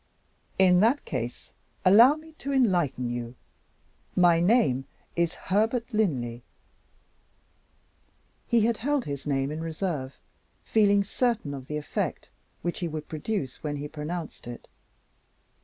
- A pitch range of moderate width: No, wide, 7.5 semitones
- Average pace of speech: No, slow, 125 wpm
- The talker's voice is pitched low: No, medium, 170 Hz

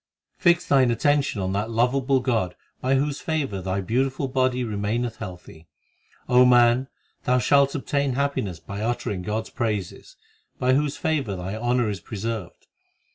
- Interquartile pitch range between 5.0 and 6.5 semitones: No, average, 4.6 semitones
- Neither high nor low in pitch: No, low, 120 Hz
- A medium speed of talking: Yes, average, 155 wpm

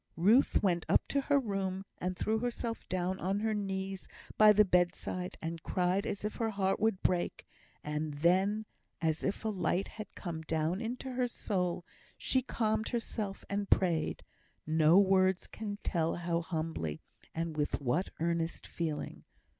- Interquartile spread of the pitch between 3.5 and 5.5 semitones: Yes, average, 4.0 semitones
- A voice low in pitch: No, high, 190 Hz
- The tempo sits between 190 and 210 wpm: No, average, 160 wpm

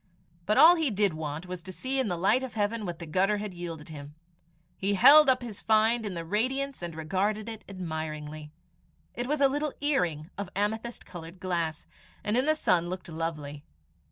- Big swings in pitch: Yes, wide, 5.9 semitones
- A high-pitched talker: Yes, high, 195 Hz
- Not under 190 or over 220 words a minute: Yes, average, 195 wpm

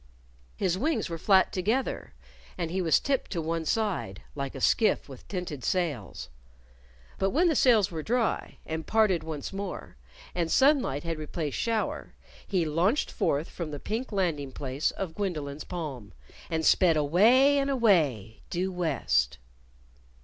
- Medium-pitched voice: Yes, medium, 175 Hz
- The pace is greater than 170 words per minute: No, average, 150 wpm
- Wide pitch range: Yes, wide, 5.9 semitones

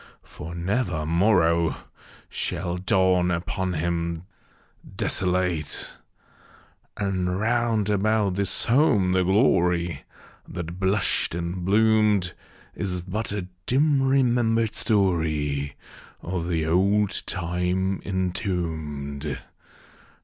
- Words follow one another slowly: Yes, slow, 90 wpm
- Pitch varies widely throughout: No, average, 3.4 semitones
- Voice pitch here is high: No, very low, 90 Hz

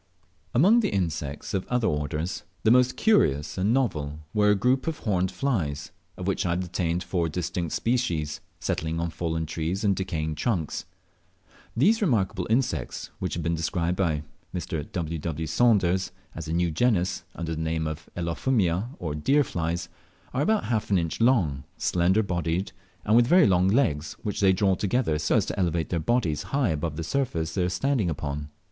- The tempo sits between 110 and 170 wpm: No, average, 180 wpm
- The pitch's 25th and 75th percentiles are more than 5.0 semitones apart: Yes, wide, 5.4 semitones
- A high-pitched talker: No, very low, 90 Hz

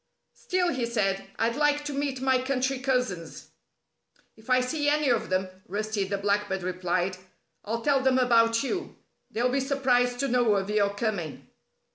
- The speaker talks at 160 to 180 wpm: Yes, average, 165 wpm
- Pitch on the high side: Yes, high, 240 Hz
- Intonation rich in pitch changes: No, average, 4.8 semitones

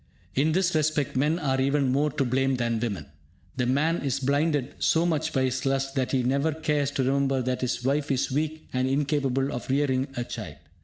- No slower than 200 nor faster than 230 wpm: Yes, fast, 205 wpm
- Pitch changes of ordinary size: No, narrow, 2.3 semitones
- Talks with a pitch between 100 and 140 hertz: Yes, low, 135 Hz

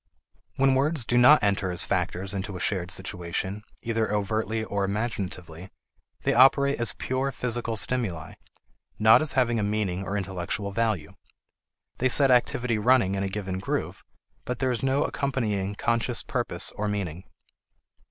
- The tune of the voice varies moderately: Yes, average, 4.3 semitones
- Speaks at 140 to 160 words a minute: Yes, average, 150 wpm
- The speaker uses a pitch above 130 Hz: No, low, 105 Hz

